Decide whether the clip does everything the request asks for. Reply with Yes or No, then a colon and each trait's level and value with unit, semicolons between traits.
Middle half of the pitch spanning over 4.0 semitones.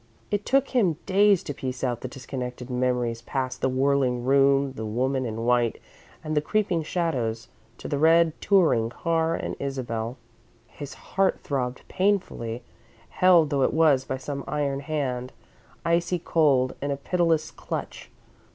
Yes: average, 4.6 semitones